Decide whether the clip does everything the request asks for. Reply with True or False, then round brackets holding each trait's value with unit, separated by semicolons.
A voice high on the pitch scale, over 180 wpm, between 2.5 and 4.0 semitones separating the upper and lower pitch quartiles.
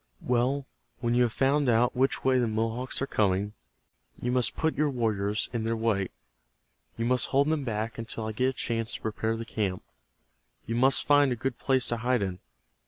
False (120 Hz; 200 wpm; 2.8 semitones)